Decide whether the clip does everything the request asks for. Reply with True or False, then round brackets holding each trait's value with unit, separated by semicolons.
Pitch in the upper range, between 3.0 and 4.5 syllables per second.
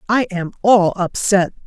True (195 Hz; 3.9 syllables/s)